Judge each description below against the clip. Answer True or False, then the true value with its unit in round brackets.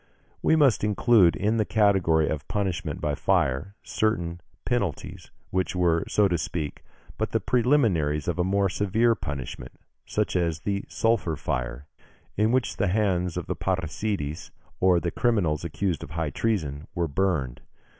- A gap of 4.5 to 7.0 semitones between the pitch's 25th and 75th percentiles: True (5.1 semitones)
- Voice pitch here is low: True (90 Hz)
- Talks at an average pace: True (150 wpm)